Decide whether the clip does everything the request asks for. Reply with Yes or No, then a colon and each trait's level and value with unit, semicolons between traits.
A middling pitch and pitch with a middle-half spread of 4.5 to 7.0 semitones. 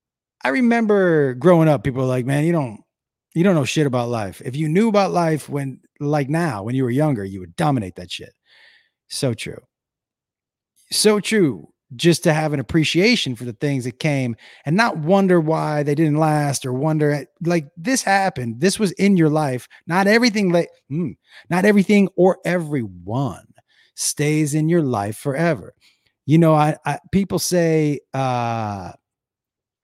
Yes: medium, 155 Hz; average, 5.1 semitones